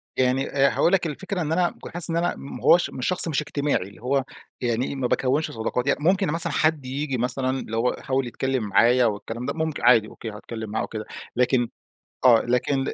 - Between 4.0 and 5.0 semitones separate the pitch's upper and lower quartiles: Yes, average, 4.4 semitones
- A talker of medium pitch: No, low, 130 Hz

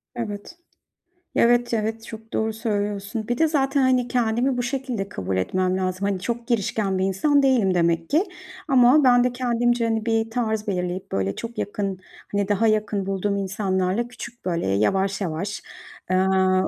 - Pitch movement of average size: Yes, average, 4.0 semitones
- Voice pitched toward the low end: No, high, 215 Hz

